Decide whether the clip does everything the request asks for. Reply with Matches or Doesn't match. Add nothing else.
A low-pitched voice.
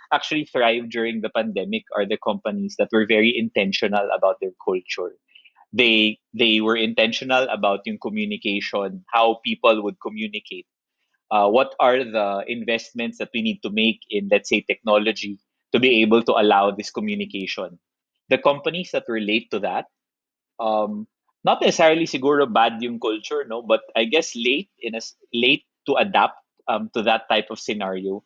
Matches